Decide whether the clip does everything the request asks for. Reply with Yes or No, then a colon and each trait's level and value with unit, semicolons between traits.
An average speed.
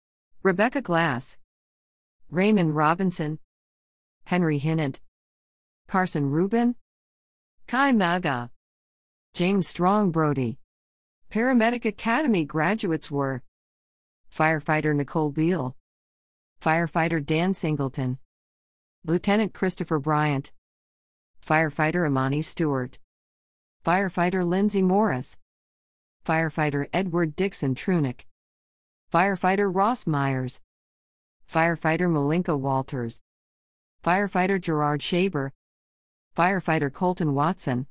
No: slow, 75 wpm